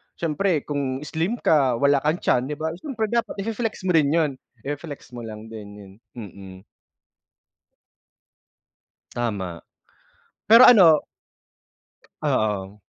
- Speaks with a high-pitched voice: No, medium, 145 Hz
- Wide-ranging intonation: Yes, wide, 7.5 semitones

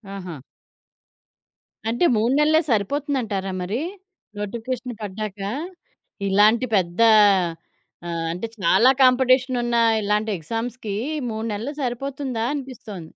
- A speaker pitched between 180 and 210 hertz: No, high, 225 Hz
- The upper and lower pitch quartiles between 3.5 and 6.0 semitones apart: Yes, average, 4.1 semitones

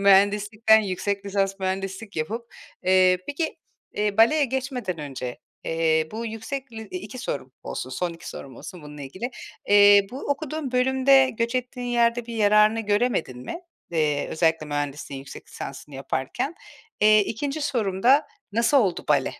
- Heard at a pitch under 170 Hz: No, high, 205 Hz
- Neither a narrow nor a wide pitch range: No, wide, 6.3 semitones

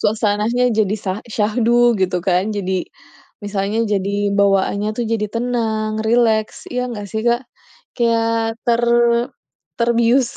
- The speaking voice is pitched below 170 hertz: No, high, 220 Hz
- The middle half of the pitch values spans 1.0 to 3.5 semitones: Yes, narrow, 2.4 semitones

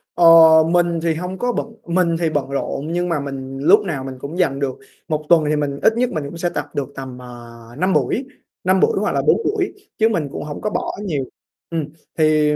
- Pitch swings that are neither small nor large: Yes, average, 4.3 semitones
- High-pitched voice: No, medium, 155 Hz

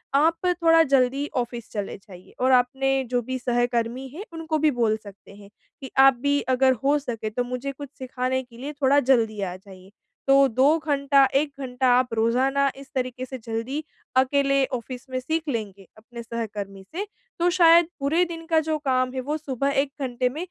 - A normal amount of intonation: Yes, average, 3.0 semitones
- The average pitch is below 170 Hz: No, very high, 260 Hz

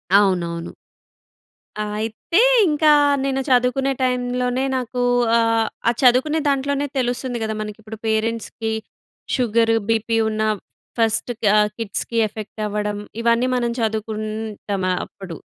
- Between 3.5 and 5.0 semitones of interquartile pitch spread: No, average, 2.8 semitones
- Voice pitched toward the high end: Yes, high, 225 Hz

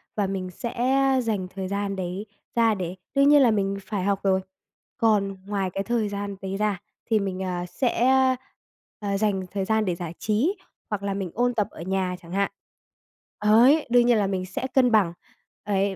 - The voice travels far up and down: No, narrow, 2.5 semitones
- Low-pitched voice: No, high, 200 Hz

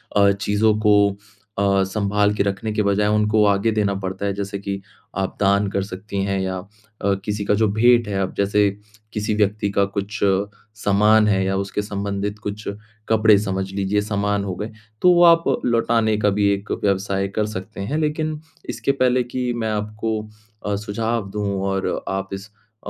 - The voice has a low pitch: Yes, low, 105 Hz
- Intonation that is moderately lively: No, narrow, 1.6 semitones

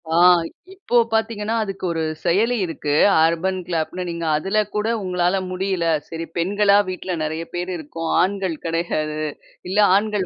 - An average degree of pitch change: Yes, average, 3.3 semitones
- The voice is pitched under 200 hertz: Yes, medium, 185 Hz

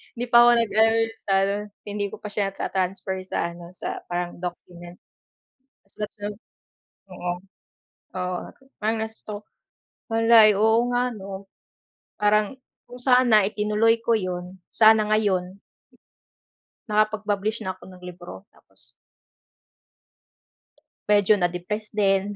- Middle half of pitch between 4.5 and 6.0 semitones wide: No, average, 2.8 semitones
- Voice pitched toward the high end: Yes, high, 205 Hz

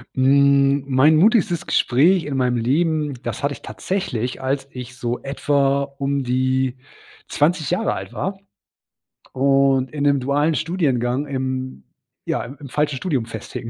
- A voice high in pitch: No, medium, 140 Hz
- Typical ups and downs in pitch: No, narrow, 2.3 semitones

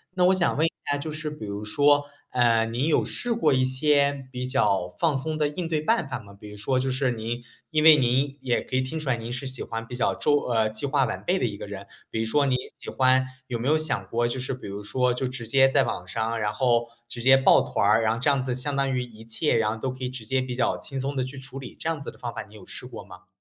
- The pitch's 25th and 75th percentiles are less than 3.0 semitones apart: No, average, 3.7 semitones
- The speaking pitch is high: No, low, 130 Hz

